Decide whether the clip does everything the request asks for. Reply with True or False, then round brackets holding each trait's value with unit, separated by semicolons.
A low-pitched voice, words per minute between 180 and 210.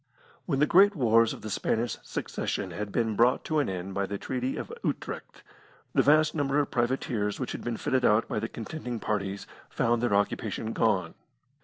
True (115 Hz; 190 wpm)